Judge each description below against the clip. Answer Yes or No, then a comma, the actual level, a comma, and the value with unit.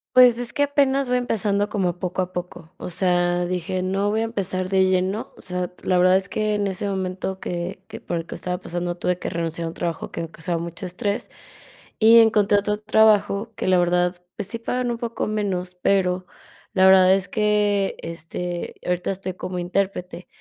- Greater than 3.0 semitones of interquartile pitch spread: No, average, 2.7 semitones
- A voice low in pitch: No, medium, 185 Hz